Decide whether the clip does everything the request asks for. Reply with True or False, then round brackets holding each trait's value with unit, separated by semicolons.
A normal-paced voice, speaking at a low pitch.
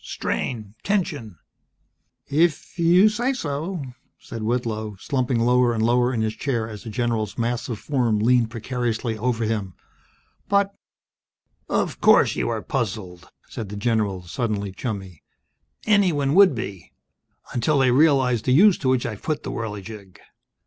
True (150 wpm; 120 Hz)